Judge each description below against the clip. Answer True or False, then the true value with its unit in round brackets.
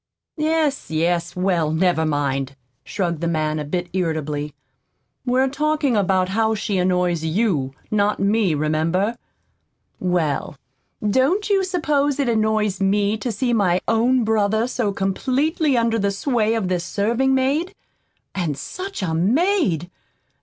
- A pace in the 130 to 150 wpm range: True (135 wpm)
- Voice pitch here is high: True (200 Hz)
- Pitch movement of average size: False (6.6 semitones)